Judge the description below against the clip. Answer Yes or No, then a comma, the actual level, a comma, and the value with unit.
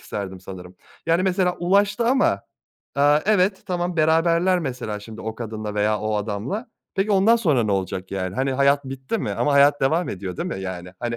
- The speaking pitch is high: No, low, 135 Hz